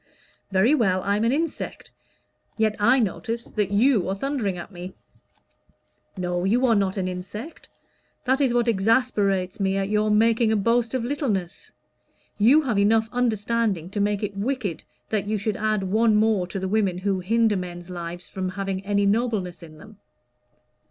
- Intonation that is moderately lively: Yes, average, 3.4 semitones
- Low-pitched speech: No, high, 205 Hz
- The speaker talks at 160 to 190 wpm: Yes, average, 170 wpm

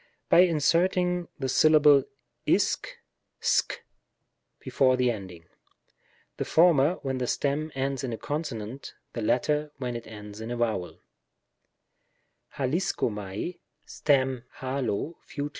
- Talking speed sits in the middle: No, slow, 110 wpm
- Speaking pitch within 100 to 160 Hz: Yes, low, 135 Hz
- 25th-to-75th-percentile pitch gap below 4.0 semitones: No, average, 4.8 semitones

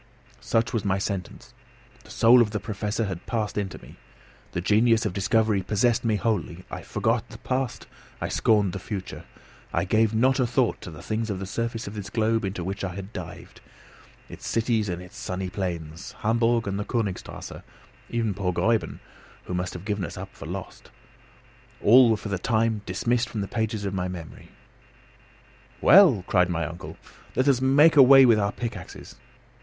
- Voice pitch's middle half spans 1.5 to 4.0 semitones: Yes, average, 3.4 semitones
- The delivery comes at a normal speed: Yes, average, 185 wpm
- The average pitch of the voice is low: Yes, low, 105 Hz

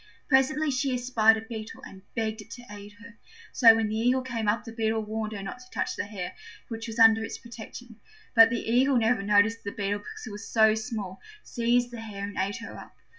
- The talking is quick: Yes, fast, 230 wpm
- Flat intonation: Yes, narrow, 2.2 semitones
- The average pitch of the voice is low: No, high, 225 Hz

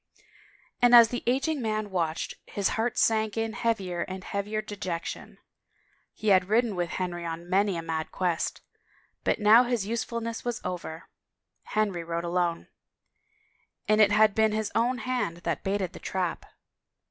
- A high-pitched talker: Yes, high, 205 Hz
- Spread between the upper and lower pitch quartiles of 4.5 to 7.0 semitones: No, average, 4.1 semitones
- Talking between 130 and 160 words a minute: Yes, average, 155 wpm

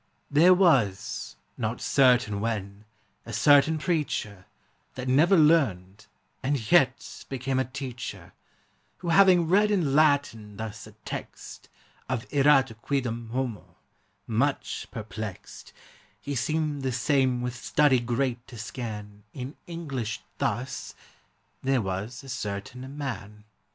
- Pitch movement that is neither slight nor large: Yes, average, 4.7 semitones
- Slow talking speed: Yes, slow, 120 wpm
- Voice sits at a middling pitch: No, low, 130 Hz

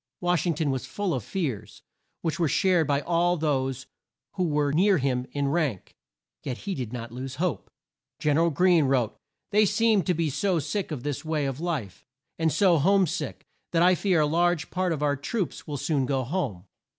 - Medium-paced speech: No, fast, 210 wpm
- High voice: No, medium, 155 Hz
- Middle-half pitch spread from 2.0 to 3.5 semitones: No, average, 4.6 semitones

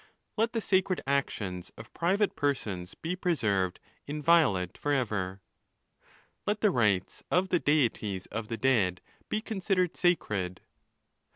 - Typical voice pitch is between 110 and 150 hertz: Yes, medium, 140 Hz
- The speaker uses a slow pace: Yes, slow, 130 wpm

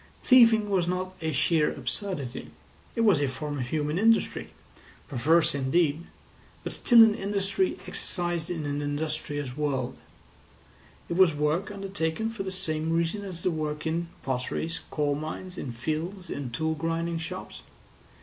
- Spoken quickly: No, average, 150 wpm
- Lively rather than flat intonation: No, average, 4.1 semitones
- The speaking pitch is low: No, medium, 165 Hz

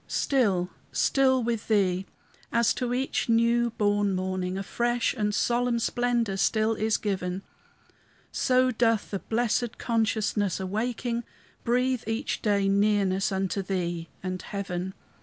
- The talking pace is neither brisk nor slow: No, slow, 125 wpm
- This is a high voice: Yes, high, 215 Hz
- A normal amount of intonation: Yes, average, 3.7 semitones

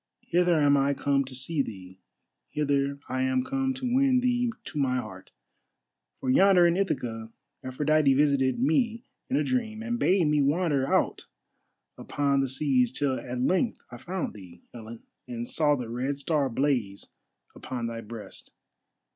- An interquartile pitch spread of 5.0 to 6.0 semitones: Yes, wide, 5.5 semitones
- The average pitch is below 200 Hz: Yes, medium, 140 Hz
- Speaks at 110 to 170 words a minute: Yes, average, 160 wpm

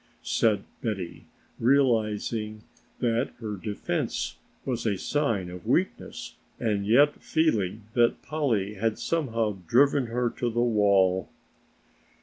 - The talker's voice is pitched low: Yes, low, 115 Hz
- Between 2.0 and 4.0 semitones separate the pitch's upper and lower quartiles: Yes, average, 3.1 semitones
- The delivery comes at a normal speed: No, slow, 115 wpm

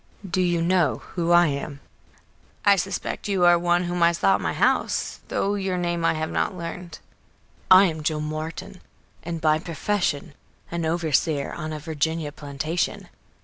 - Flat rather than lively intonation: Yes, narrow, 2.3 semitones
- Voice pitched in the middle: Yes, medium, 170 Hz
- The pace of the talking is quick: No, average, 165 wpm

